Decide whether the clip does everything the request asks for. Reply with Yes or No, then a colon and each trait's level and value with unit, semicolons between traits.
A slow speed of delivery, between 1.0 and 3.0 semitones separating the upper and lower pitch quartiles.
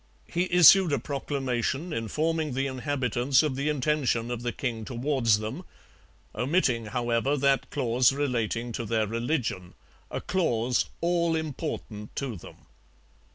No: slow, 130 wpm; average, 4.4 semitones